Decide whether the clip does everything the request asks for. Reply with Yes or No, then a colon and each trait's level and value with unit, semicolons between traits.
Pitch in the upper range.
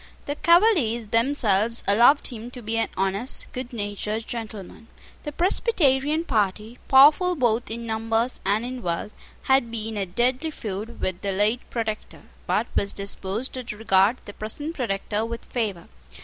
Yes: high, 230 Hz